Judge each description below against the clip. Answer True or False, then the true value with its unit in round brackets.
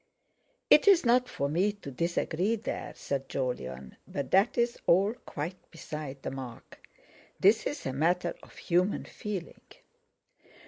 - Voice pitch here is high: False (175 Hz)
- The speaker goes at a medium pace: False (130 wpm)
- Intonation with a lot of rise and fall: True (7.2 semitones)